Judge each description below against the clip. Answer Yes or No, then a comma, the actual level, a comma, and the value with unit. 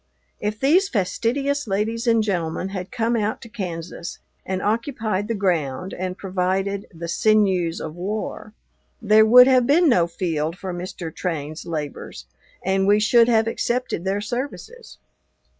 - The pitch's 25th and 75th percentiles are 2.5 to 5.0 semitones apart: Yes, average, 4.3 semitones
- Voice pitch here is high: Yes, high, 200 Hz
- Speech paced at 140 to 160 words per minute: Yes, average, 145 wpm